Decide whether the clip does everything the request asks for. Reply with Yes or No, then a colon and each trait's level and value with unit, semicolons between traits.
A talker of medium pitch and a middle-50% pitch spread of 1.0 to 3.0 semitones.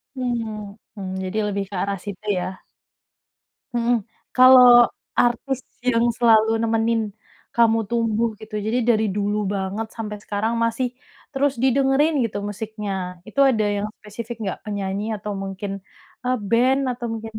No: high, 225 Hz; narrow, 2.6 semitones